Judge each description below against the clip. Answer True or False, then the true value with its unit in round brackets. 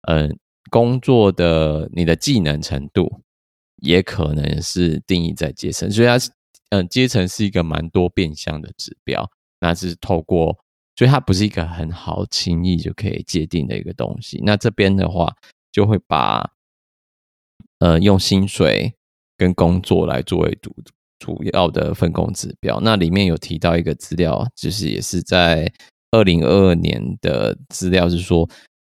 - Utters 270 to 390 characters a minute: False (235 characters per minute)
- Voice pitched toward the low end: True (90 Hz)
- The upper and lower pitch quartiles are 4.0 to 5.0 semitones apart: False (3.4 semitones)